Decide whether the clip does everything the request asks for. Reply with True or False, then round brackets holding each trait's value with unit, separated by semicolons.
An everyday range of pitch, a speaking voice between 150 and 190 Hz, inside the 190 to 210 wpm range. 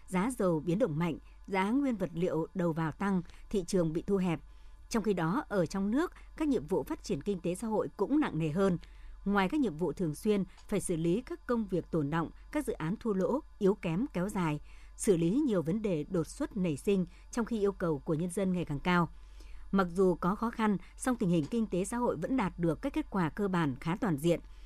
False (4.2 semitones; 185 Hz; 245 wpm)